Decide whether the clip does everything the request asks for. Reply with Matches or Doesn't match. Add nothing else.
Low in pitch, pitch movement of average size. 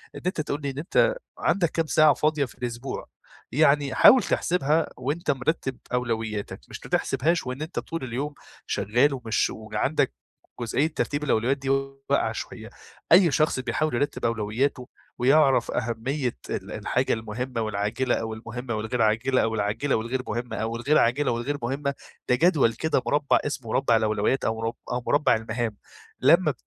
Matches